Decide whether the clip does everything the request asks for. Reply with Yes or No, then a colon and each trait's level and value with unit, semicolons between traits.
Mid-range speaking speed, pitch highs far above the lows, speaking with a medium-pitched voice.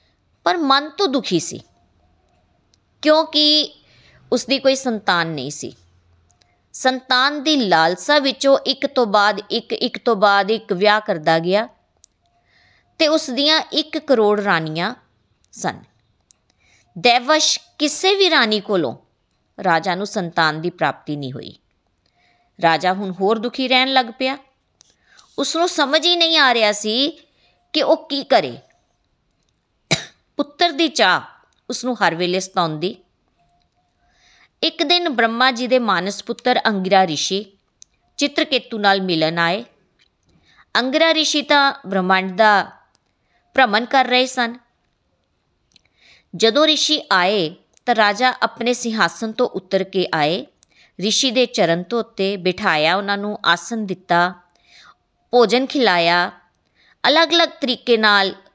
No: average, 125 wpm; wide, 6.9 semitones; high, 225 Hz